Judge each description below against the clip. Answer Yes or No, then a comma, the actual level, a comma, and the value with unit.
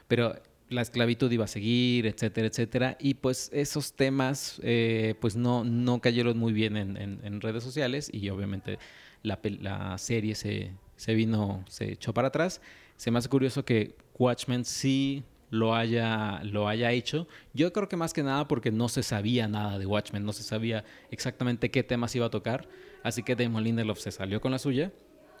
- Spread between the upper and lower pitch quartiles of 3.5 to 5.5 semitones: No, average, 3.0 semitones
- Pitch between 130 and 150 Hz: No, low, 115 Hz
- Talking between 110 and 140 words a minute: No, average, 185 wpm